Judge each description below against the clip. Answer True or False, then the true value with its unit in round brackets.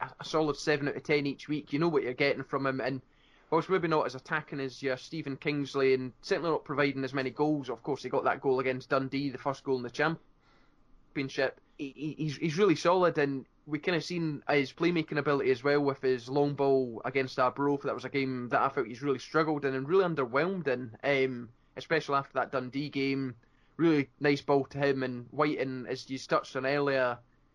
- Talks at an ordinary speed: False (220 wpm)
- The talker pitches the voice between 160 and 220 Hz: False (140 Hz)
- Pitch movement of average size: False (2.3 semitones)